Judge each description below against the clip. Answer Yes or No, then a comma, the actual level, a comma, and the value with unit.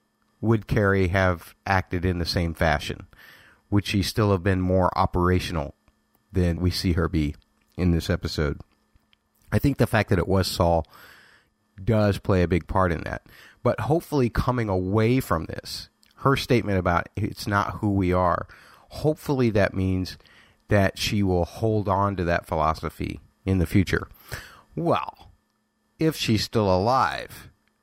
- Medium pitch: No, very low, 95 Hz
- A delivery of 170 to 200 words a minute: No, average, 155 wpm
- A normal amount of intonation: Yes, average, 3.5 semitones